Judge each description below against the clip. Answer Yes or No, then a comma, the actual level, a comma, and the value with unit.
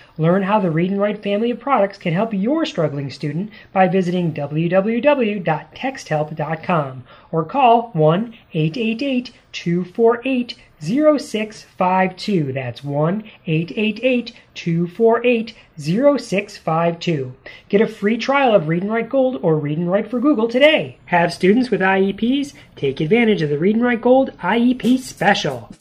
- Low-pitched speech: No, high, 200 Hz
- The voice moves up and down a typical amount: No, wide, 6.1 semitones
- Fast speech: No, slow, 135 wpm